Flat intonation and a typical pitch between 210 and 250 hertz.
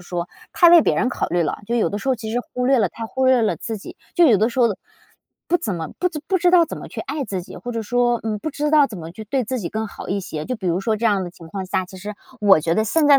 No: average, 5.2 semitones; high, 225 Hz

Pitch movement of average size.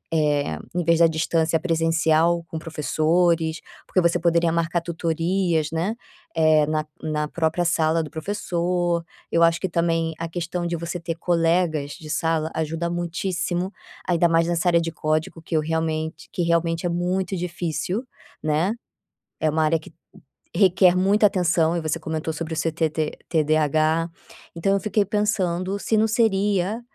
No: narrow, 1.8 semitones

